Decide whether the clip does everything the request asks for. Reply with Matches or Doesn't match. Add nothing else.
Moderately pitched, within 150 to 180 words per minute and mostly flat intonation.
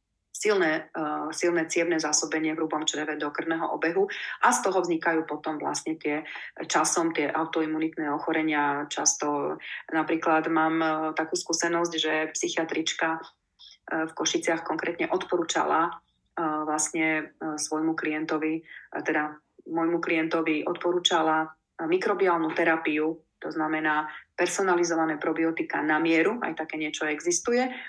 Doesn't match